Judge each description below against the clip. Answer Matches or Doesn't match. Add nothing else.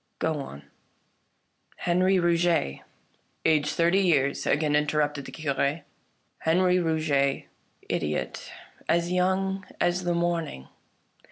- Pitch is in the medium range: Matches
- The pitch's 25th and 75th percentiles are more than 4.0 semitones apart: Doesn't match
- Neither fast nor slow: Doesn't match